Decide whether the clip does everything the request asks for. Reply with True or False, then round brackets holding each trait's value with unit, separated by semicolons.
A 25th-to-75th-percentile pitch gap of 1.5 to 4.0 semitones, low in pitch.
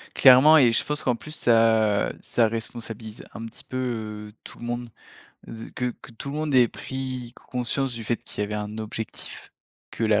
True (2.5 semitones; 115 Hz)